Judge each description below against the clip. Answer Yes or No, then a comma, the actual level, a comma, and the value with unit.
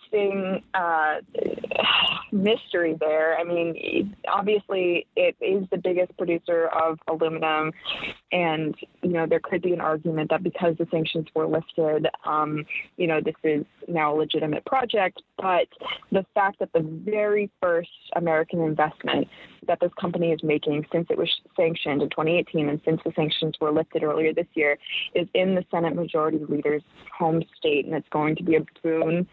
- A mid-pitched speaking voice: Yes, medium, 165 Hz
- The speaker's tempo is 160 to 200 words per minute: Yes, average, 165 wpm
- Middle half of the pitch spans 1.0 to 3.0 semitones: Yes, narrow, 2.5 semitones